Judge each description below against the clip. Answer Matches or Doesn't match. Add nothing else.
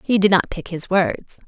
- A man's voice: Doesn't match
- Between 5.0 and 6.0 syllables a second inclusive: Doesn't match